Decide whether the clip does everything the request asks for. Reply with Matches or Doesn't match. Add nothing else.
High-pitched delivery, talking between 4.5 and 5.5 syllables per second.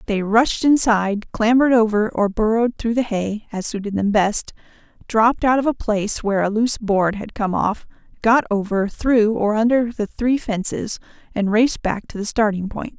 Matches